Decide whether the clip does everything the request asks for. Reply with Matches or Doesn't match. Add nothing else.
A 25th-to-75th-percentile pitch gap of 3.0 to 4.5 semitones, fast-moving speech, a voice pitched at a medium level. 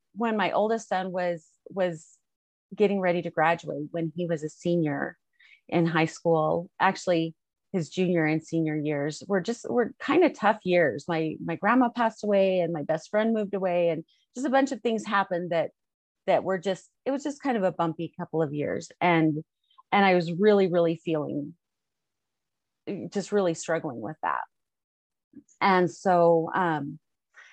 Doesn't match